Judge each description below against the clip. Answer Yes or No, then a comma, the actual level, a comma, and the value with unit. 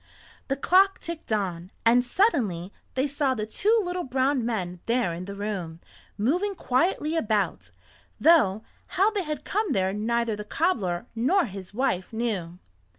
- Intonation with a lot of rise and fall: Yes, wide, 8.3 semitones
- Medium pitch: No, high, 235 Hz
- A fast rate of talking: No, average, 155 wpm